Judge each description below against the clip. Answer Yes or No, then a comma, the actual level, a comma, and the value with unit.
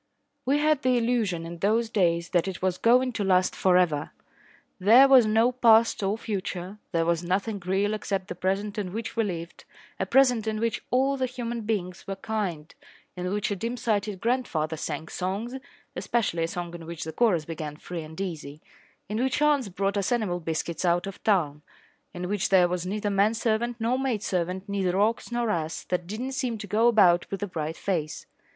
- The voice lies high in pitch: Yes, high, 200 Hz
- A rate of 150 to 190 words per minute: No, average, 200 wpm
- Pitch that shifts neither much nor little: Yes, average, 4.5 semitones